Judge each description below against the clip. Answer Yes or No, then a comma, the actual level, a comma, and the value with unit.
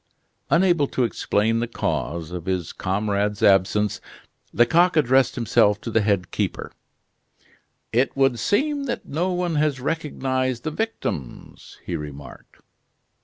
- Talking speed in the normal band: No, slow, 125 wpm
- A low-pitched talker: Yes, low, 120 Hz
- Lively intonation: Yes, wide, 7.3 semitones